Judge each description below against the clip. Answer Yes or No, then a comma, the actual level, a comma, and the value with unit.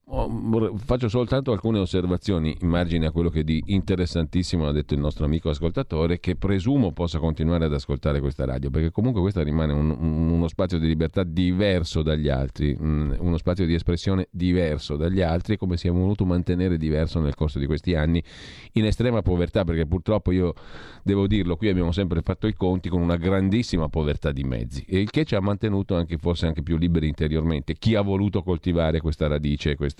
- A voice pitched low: Yes, very low, 85 Hz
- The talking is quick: Yes, fast, 190 wpm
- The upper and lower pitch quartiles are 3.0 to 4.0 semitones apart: Yes, average, 3.5 semitones